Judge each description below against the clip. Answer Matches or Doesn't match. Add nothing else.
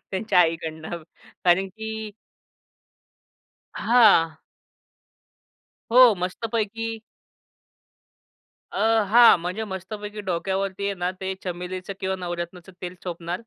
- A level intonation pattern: Doesn't match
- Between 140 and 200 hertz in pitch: Matches